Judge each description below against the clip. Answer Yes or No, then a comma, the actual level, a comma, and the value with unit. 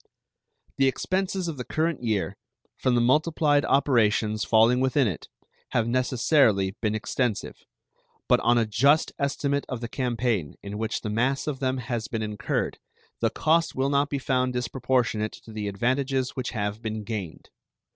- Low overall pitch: Yes, low, 125 Hz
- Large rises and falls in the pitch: No, average, 3.9 semitones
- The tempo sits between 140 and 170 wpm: Yes, average, 160 wpm